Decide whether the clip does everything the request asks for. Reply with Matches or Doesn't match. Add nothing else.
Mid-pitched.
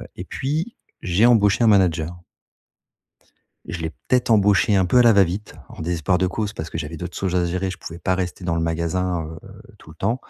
Doesn't match